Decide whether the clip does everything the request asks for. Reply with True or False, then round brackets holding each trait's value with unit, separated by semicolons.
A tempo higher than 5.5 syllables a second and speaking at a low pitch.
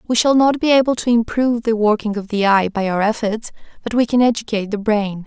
False (6.0 syllables/s; 225 Hz)